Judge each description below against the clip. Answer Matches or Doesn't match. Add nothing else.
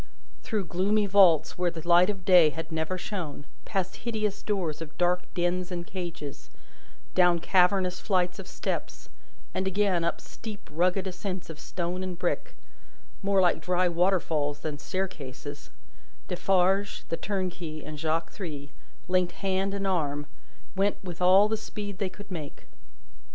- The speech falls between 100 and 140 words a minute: Doesn't match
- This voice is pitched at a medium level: Matches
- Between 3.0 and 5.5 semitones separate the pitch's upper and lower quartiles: Doesn't match